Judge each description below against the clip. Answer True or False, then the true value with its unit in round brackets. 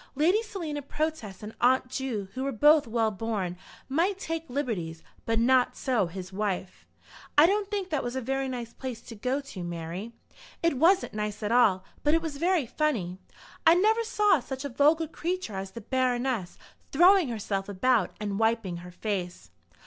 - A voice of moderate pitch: False (250 Hz)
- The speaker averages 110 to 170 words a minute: False (180 wpm)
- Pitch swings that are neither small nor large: False (6.9 semitones)